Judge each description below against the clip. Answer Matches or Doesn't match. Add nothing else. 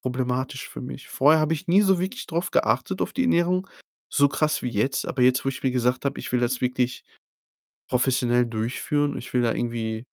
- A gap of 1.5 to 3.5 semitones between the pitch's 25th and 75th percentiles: Doesn't match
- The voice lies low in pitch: Matches